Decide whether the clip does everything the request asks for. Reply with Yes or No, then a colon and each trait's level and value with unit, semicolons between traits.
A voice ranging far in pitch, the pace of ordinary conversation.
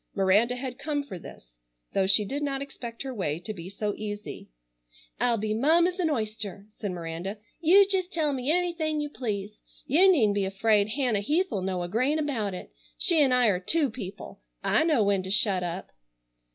Yes: wide, 6.8 semitones; average, 190 wpm